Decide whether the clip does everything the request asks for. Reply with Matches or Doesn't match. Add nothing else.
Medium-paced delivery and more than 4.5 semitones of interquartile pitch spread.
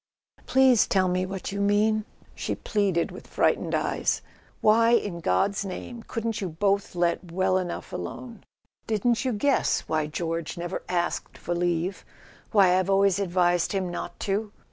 Doesn't match